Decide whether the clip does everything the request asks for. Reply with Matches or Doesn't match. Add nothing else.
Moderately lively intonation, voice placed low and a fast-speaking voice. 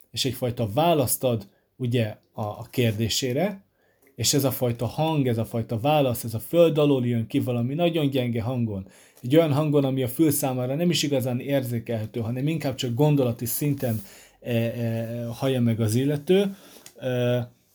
Matches